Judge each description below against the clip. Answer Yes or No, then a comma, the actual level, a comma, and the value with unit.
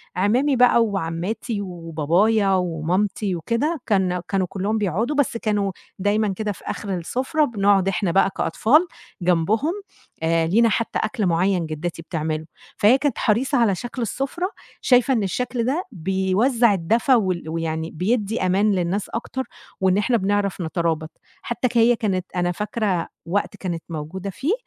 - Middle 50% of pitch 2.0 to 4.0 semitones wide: No, average, 4.7 semitones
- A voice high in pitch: Yes, high, 200 Hz